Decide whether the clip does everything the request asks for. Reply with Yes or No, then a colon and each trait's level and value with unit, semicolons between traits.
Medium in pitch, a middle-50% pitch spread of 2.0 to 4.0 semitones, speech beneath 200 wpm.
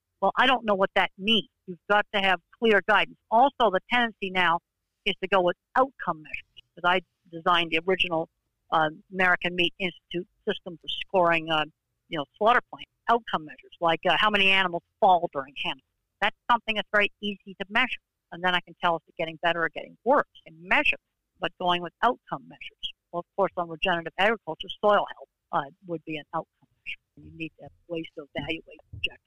No: medium, 180 Hz; average, 3.7 semitones; fast, 205 wpm